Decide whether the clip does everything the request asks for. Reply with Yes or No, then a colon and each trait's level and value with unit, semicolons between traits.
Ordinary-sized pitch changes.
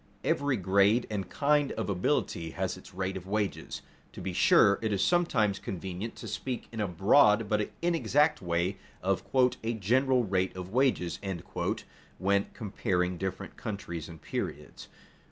Yes: average, 3.9 semitones